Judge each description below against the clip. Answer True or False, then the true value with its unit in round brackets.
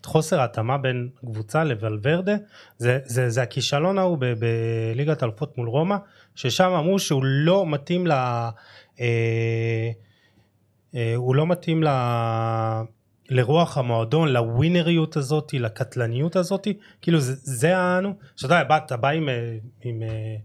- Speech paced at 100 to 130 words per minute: True (125 wpm)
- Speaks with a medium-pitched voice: False (130 Hz)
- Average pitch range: False (5.7 semitones)